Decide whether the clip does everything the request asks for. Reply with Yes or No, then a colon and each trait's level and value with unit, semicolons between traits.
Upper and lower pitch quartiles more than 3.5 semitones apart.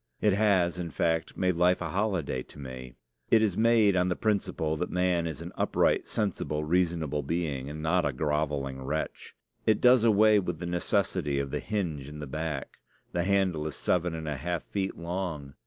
Yes: average, 3.9 semitones